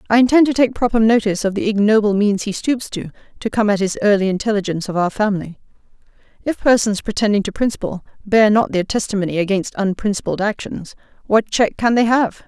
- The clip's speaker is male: No, female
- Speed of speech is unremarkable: Yes, average, 190 wpm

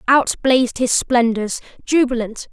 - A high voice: Yes, high, 245 Hz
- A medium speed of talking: No, slow, 95 wpm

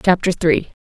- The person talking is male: No, female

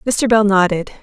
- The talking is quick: No, average, 175 wpm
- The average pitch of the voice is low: No, high, 210 Hz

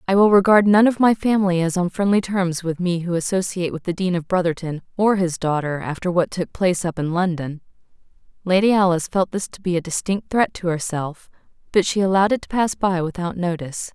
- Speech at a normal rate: No, fast, 215 wpm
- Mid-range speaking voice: Yes, medium, 180 Hz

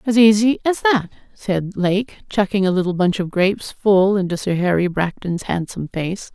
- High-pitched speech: Yes, high, 195 Hz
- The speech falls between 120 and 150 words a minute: No, average, 180 wpm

